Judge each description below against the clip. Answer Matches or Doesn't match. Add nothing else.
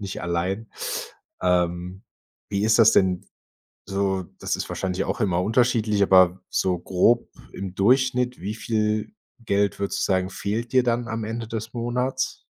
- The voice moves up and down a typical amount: Matches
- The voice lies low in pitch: Matches